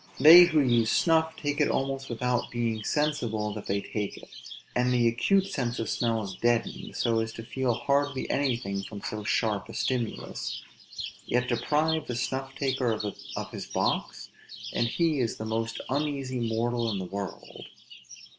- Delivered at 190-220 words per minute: No, average, 165 wpm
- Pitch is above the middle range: No, low, 120 Hz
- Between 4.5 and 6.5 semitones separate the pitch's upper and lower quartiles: No, average, 3.6 semitones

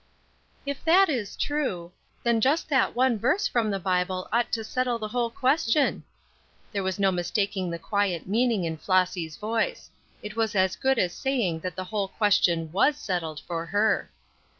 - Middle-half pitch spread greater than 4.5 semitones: Yes, average, 5.1 semitones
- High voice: Yes, high, 210 Hz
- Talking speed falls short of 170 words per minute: No, average, 175 wpm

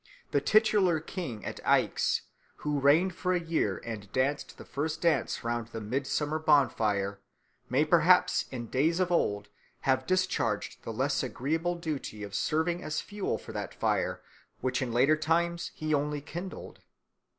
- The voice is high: No, medium, 145 Hz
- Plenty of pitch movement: Yes, wide, 6.1 semitones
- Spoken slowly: No, average, 155 wpm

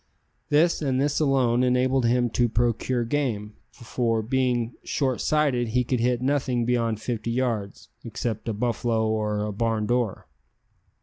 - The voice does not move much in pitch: Yes, narrow, 2.3 semitones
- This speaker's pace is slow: No, average, 145 wpm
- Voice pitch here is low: Yes, low, 120 Hz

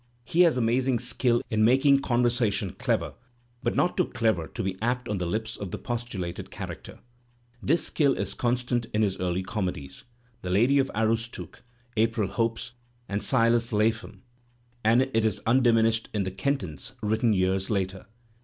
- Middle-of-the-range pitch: No, low, 115 Hz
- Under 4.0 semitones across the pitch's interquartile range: Yes, average, 3.6 semitones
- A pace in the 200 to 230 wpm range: No, average, 170 wpm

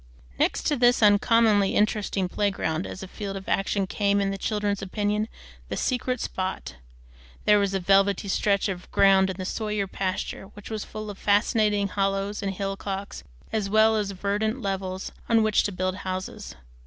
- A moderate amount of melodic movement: No, narrow, 1.6 semitones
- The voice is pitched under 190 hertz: No, high, 200 Hz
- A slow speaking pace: No, average, 170 wpm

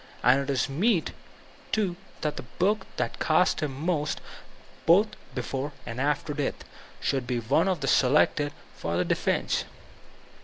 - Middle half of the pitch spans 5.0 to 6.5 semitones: No, average, 4.3 semitones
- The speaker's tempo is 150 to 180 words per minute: No, average, 140 wpm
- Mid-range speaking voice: Yes, medium, 145 Hz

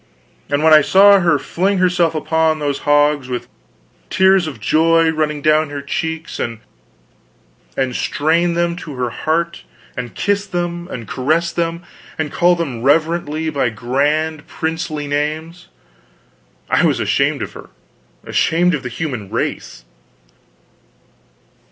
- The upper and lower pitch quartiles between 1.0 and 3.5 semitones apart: Yes, average, 3.0 semitones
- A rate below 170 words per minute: Yes, slow, 135 wpm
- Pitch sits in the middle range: Yes, medium, 155 Hz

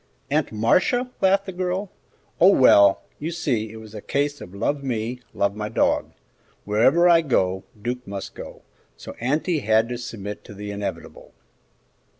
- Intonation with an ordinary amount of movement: No, wide, 8.0 semitones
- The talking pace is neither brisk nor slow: Yes, average, 160 wpm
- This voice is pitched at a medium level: No, low, 120 Hz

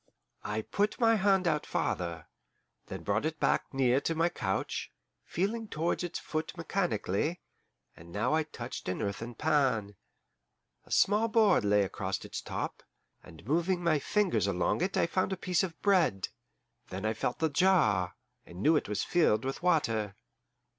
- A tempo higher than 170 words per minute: No, average, 165 wpm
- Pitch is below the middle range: No, medium, 150 Hz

